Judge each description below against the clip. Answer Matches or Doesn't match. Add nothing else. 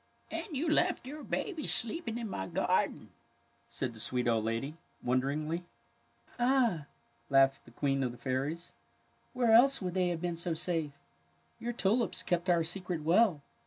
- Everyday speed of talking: Matches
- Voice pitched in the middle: Matches